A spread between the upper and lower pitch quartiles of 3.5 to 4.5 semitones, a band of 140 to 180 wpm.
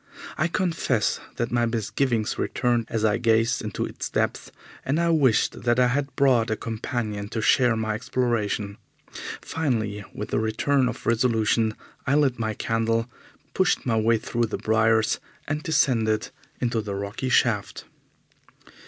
No: narrow, 2.6 semitones; average, 150 wpm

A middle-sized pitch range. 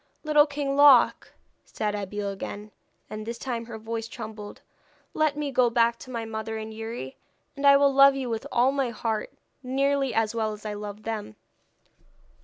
Yes: average, 4.1 semitones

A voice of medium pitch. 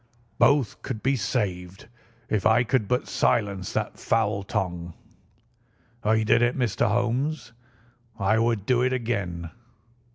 No: low, 110 Hz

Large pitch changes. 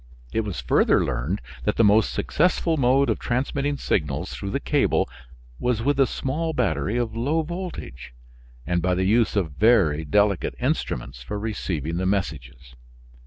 Yes: wide, 7.2 semitones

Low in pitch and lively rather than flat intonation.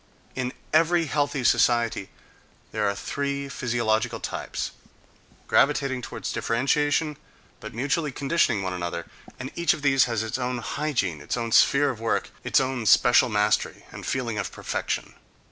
No: low, 125 Hz; average, 4.0 semitones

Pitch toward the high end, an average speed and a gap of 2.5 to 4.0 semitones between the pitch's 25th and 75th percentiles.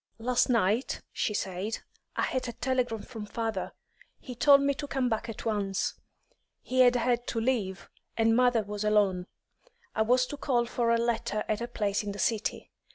Yes: high, 230 Hz; average, 185 wpm; average, 2.9 semitones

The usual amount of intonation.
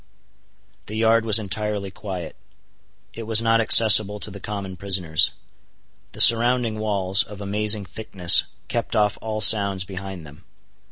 No: narrow, 2.2 semitones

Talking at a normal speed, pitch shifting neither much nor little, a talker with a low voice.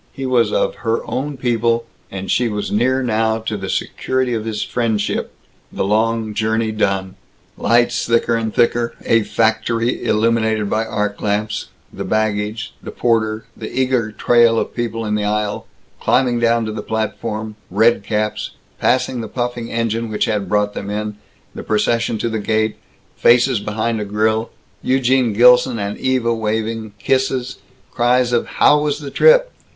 No: average, 160 wpm; narrow, 2.0 semitones; low, 115 Hz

